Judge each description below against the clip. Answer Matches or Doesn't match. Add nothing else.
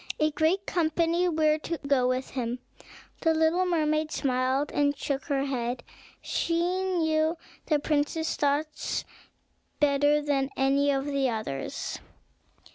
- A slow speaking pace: Matches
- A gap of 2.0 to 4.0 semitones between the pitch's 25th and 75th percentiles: Matches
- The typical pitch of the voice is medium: Doesn't match